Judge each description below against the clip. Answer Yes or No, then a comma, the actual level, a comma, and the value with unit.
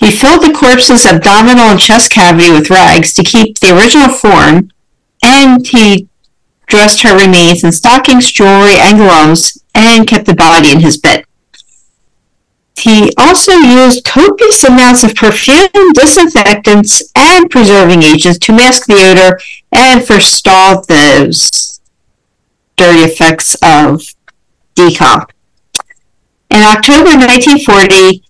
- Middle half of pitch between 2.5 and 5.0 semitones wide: No, wide, 5.4 semitones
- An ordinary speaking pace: No, slow, 120 wpm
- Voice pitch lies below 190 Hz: No, high, 210 Hz